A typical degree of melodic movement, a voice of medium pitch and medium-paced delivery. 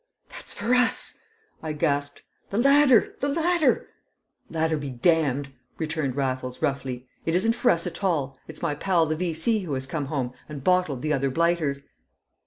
Yes: average, 4.8 semitones; medium, 155 Hz; average, 170 wpm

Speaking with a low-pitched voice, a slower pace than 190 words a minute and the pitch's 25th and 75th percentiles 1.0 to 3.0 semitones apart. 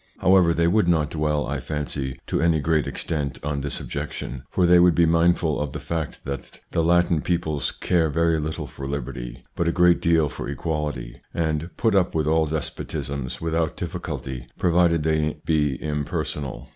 Yes: very low, 80 Hz; average, 180 wpm; narrow, 2.6 semitones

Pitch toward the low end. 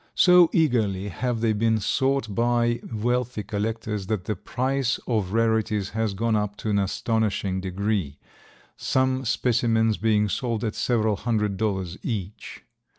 Yes: low, 110 Hz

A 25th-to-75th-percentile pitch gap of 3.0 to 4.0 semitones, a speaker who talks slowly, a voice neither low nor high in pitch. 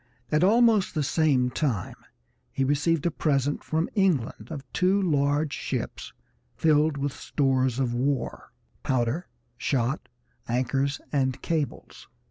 Yes: average, 3.3 semitones; slow, 120 wpm; medium, 145 Hz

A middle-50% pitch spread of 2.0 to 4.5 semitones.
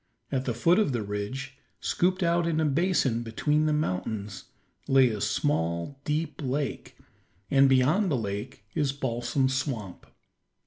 No: average, 4.9 semitones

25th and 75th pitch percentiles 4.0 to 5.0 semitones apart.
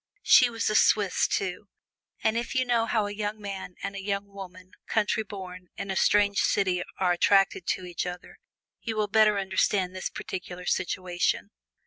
No: narrow, 2.4 semitones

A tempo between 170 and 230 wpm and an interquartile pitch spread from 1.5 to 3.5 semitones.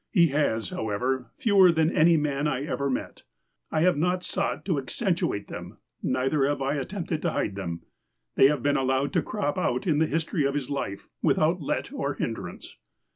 No: average, 190 wpm; average, 4.0 semitones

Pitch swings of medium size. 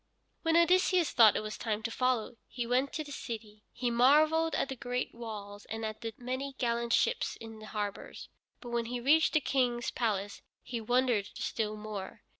Yes: average, 3.5 semitones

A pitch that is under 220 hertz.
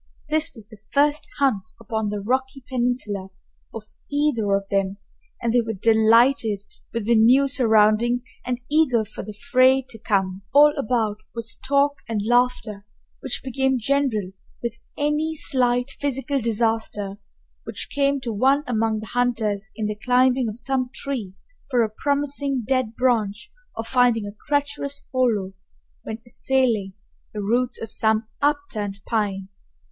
No: high, 235 Hz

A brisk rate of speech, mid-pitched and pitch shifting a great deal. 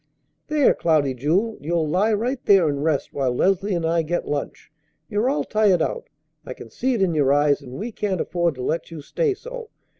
Yes: fast, 210 wpm; medium, 175 Hz; wide, 6.5 semitones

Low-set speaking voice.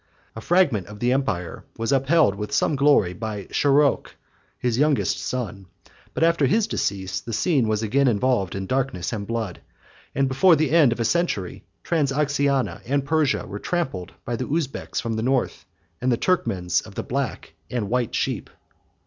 Yes: low, 125 Hz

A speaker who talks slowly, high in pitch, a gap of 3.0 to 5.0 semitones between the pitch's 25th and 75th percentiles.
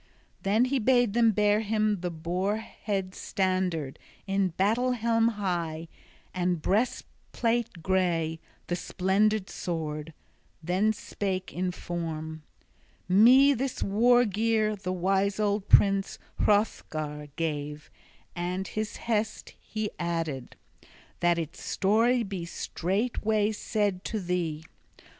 Yes: slow, 110 wpm; high, 195 Hz; average, 3.9 semitones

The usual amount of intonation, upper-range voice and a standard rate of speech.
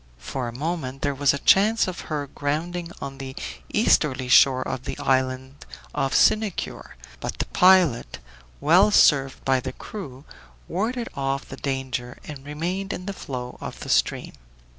No: average, 5.0 semitones; medium, 140 Hz; average, 160 wpm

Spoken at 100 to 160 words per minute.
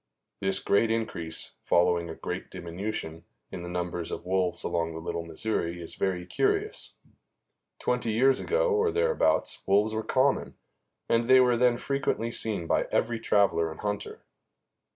Yes: average, 150 wpm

